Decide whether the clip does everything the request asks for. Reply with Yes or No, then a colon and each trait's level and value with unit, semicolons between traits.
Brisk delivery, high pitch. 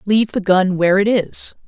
Yes: fast, 215 wpm; high, 200 Hz